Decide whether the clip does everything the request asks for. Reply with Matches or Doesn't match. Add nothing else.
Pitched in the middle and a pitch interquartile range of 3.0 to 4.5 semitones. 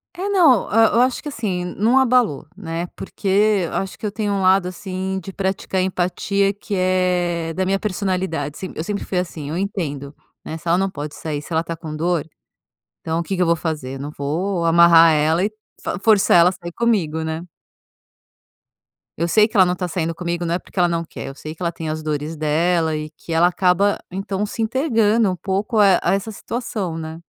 Matches